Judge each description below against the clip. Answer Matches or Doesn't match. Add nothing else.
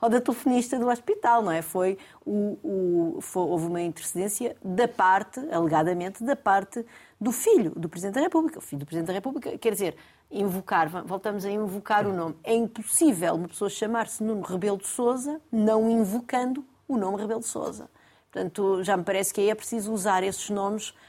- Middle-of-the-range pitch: Doesn't match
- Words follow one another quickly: Matches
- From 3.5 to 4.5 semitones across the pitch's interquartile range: Matches